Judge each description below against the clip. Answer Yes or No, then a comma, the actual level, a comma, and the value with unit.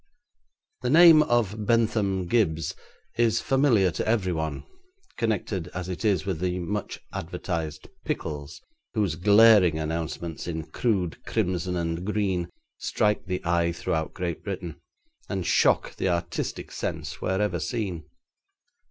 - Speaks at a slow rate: Yes, slow, 125 wpm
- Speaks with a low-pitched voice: Yes, very low, 90 Hz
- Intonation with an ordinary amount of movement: Yes, average, 3.9 semitones